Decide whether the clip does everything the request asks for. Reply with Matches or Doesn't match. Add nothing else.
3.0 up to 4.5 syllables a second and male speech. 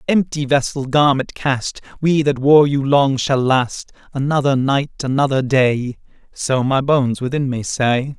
Matches